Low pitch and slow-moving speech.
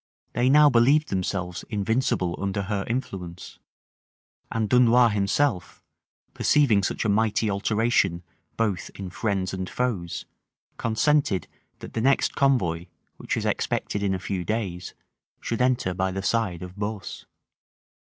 Yes: low, 105 Hz; slow, 130 wpm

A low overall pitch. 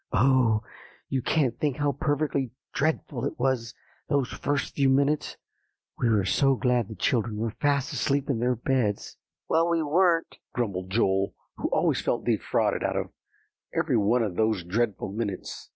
Yes: low, 125 Hz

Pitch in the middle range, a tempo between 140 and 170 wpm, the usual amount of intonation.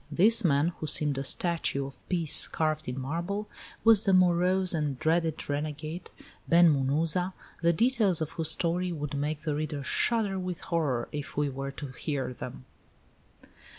Yes: medium, 160 Hz; average, 160 wpm; average, 3.8 semitones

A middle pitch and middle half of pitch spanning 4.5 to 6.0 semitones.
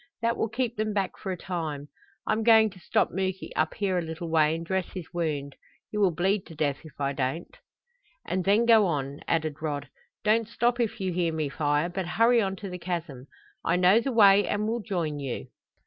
Yes: medium, 180 Hz; average, 4.9 semitones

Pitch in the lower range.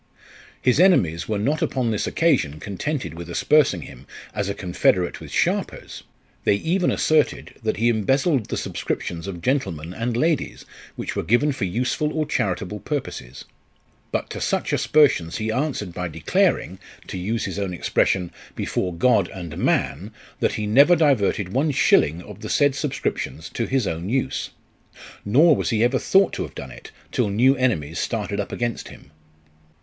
Yes: low, 110 Hz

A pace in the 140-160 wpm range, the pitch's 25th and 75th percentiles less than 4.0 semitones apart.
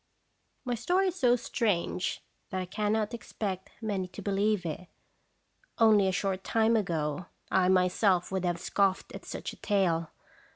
Yes: average, 155 wpm; average, 3.2 semitones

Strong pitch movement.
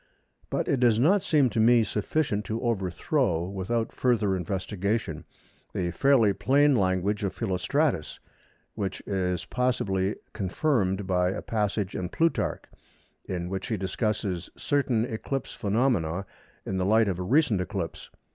No: average, 4.6 semitones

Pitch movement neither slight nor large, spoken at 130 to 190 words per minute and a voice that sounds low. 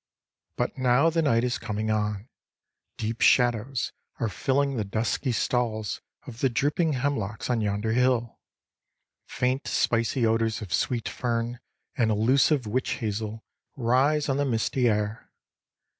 Yes: average, 3.0 semitones; slow, 135 wpm; low, 120 Hz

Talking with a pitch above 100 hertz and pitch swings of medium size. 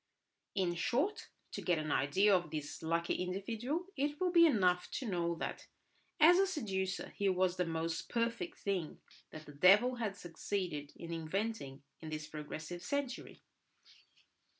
No: medium, 185 Hz; wide, 6.3 semitones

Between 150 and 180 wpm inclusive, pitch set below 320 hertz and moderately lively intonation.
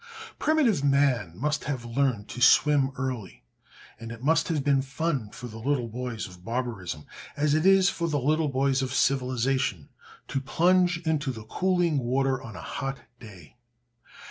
Yes: average, 165 wpm; low, 135 Hz; average, 4.3 semitones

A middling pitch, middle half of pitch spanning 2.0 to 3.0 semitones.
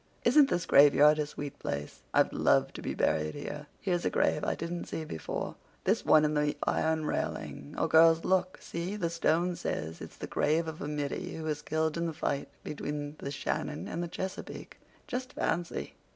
Yes: medium, 160 Hz; narrow, 2.5 semitones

